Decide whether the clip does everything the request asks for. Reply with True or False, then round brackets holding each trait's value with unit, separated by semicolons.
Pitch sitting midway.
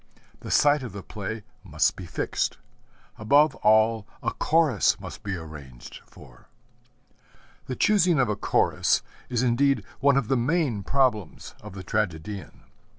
False (110 Hz)